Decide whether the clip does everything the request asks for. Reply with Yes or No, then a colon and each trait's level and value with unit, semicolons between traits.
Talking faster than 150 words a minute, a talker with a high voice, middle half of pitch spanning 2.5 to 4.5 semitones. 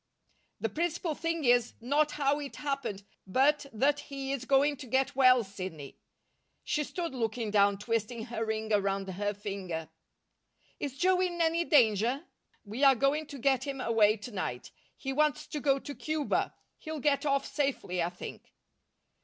No: average, 165 wpm; very high, 265 Hz; average, 5.3 semitones